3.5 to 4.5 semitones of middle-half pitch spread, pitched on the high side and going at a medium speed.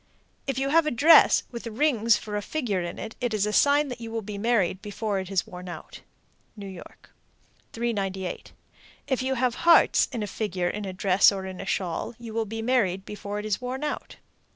No: average, 4.2 semitones; high, 215 Hz; fast, 210 wpm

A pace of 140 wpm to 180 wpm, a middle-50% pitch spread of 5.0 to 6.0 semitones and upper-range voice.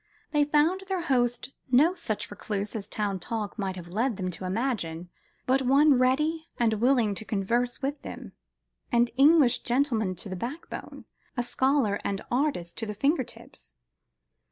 Yes: average, 160 wpm; wide, 5.4 semitones; high, 240 Hz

